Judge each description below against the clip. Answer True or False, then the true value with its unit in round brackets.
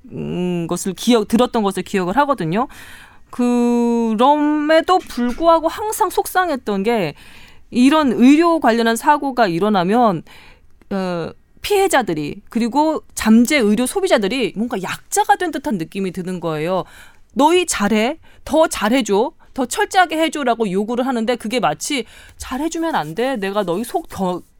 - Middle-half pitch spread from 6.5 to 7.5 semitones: True (7.1 semitones)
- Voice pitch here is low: False (245 Hz)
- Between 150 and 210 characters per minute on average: False (290 characters per minute)